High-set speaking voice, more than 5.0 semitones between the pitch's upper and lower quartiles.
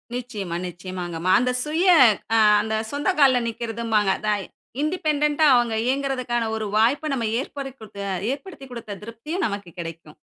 Yes: high, 235 Hz; wide, 5.4 semitones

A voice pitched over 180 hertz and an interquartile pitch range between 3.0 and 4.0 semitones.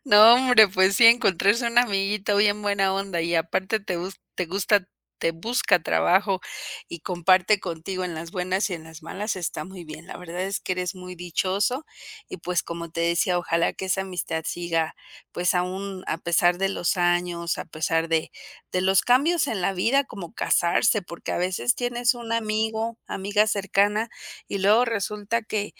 Yes: high, 190 Hz; average, 3.3 semitones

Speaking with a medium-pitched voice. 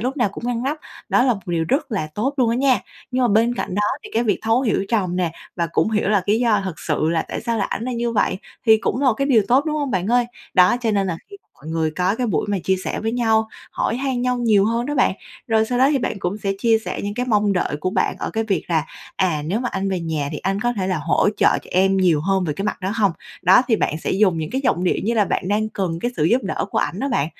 No: high, 210 Hz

